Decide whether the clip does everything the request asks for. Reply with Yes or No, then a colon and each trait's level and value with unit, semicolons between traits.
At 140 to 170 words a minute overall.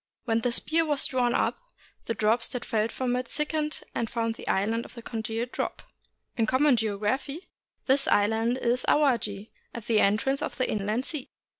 No: average, 185 wpm